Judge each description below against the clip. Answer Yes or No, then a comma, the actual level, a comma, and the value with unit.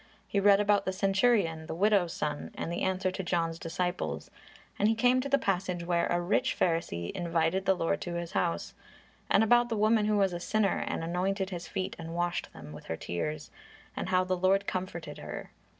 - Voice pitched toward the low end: No, medium, 185 Hz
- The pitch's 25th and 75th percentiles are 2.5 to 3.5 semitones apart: Yes, average, 3.0 semitones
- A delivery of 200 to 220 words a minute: Yes, fast, 205 wpm